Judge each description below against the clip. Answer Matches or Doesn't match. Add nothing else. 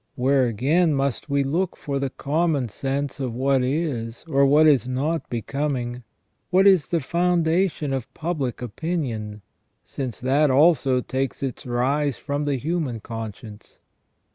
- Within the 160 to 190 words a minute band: Doesn't match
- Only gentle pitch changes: Doesn't match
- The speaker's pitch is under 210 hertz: Matches